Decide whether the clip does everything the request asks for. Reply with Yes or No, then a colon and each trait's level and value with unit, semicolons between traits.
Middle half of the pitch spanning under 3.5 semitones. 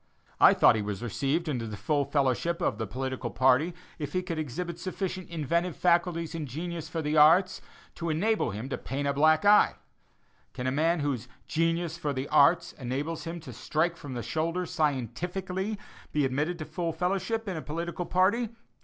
No: average, 3.9 semitones